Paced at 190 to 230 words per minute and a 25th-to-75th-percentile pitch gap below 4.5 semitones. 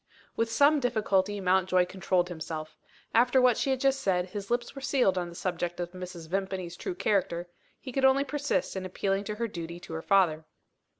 No: average, 195 wpm; wide, 5.5 semitones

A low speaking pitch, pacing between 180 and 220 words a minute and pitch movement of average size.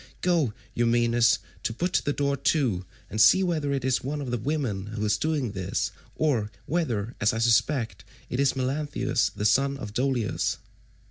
No: low, 130 Hz; average, 170 wpm; average, 4.6 semitones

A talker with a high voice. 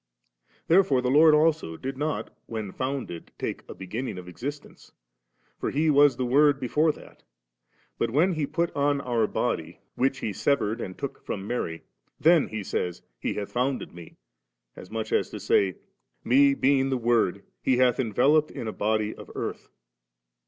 No: low, 130 Hz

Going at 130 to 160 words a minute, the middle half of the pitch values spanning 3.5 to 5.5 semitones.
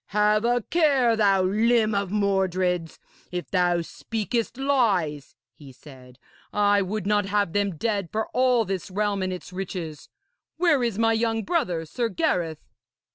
Yes: average, 150 wpm; average, 4.1 semitones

